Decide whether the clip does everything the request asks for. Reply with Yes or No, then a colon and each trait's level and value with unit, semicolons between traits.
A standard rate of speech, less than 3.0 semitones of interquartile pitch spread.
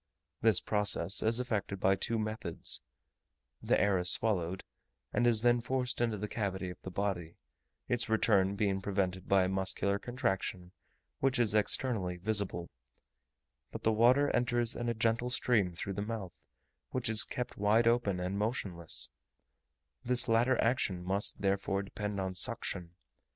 No: average, 150 wpm; average, 3.6 semitones